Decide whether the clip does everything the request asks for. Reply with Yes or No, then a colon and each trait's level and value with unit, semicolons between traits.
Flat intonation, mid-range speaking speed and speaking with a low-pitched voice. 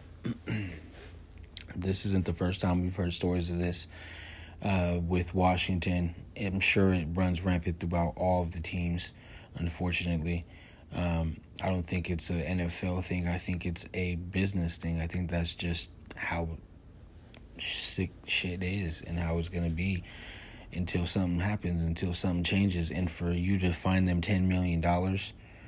Yes: narrow, 1.5 semitones; average, 155 wpm; very low, 90 Hz